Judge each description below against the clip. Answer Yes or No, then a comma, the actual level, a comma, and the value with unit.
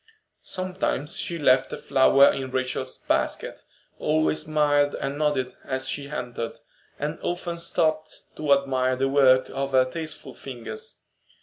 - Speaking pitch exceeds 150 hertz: No, medium, 140 Hz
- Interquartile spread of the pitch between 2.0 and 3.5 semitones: Yes, average, 3.0 semitones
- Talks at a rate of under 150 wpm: Yes, slow, 135 wpm